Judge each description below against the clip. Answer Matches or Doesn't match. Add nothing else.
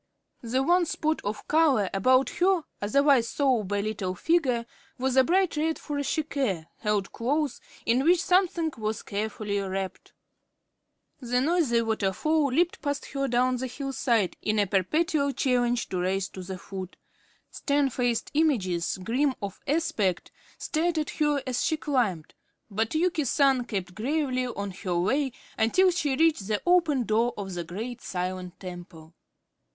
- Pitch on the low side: Doesn't match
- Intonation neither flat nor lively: Doesn't match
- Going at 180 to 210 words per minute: Doesn't match